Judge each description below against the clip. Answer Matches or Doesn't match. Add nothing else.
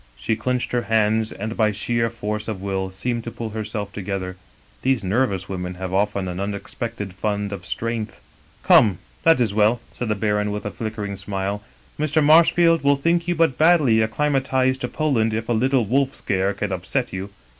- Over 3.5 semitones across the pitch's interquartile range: Matches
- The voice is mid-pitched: Doesn't match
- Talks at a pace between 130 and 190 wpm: Doesn't match